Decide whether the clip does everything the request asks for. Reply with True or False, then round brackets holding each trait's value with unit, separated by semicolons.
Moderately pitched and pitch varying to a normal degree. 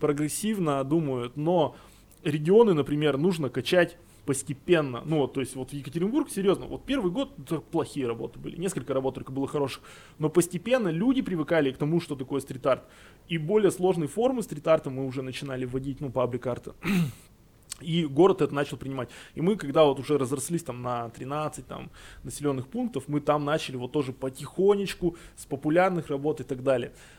True (145 Hz; 4.2 semitones)